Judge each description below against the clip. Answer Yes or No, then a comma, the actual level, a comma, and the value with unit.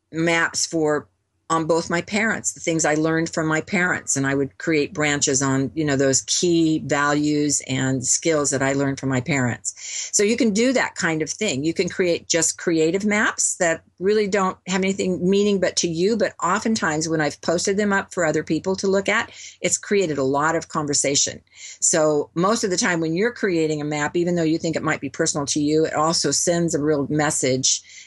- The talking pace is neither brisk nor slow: No, fast, 215 wpm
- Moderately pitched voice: Yes, medium, 160 Hz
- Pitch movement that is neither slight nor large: Yes, average, 3.7 semitones